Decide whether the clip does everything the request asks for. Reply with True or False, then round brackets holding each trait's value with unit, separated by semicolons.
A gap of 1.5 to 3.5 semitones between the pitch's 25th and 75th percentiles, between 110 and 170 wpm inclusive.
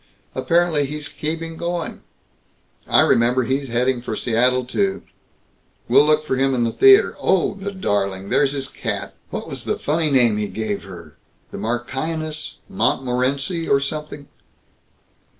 False (4.8 semitones; 145 wpm)